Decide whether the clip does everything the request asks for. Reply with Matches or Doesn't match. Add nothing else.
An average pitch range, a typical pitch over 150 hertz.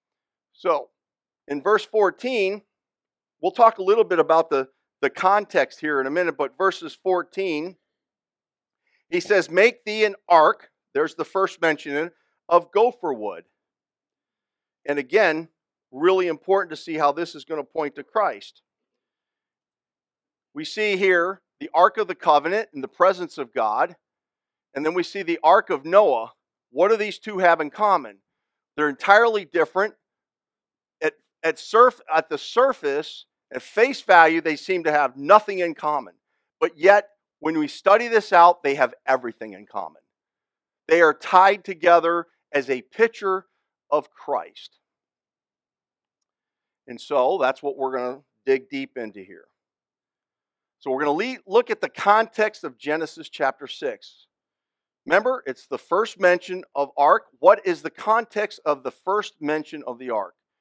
Doesn't match